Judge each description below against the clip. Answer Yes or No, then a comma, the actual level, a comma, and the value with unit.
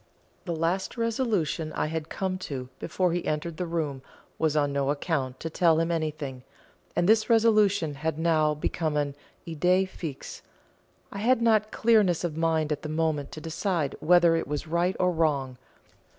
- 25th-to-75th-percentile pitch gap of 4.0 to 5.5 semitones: No, average, 3.3 semitones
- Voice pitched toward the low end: No, medium, 165 Hz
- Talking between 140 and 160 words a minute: No, average, 170 wpm